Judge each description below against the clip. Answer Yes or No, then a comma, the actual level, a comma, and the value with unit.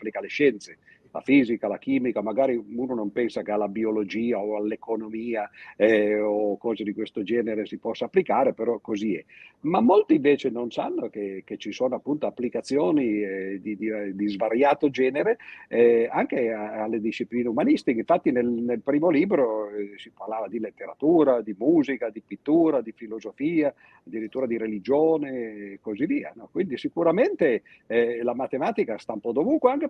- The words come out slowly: No, fast, 170 wpm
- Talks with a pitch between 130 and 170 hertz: No, low, 115 Hz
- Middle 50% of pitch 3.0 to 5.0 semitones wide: Yes, average, 4.2 semitones